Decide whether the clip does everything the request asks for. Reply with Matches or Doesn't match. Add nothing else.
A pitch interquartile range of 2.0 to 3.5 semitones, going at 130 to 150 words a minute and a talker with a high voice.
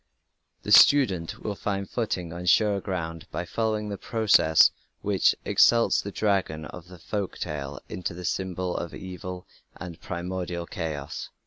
Doesn't match